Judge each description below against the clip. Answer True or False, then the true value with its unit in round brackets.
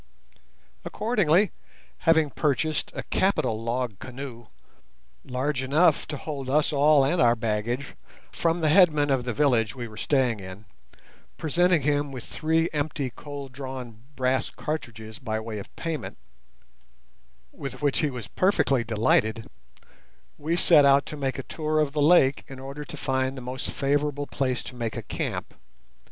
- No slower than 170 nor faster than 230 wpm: False (155 wpm)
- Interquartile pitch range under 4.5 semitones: True (3.6 semitones)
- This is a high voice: False (135 Hz)